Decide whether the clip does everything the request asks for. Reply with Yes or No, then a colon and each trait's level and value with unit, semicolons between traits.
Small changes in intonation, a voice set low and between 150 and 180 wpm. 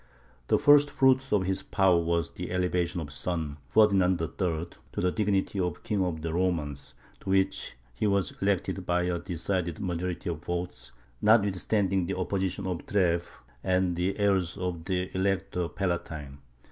Yes: narrow, 2.2 semitones; very low, 90 Hz; average, 165 wpm